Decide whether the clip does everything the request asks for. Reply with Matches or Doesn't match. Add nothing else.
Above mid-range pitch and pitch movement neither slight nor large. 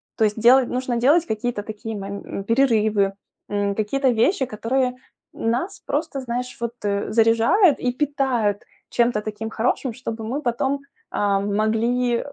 Matches